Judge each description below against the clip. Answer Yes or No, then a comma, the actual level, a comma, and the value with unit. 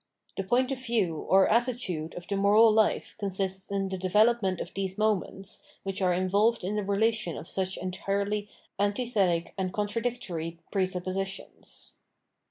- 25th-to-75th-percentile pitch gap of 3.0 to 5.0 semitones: No, narrow, 2.6 semitones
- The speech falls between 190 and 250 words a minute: No, average, 150 wpm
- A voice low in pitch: No, high, 195 Hz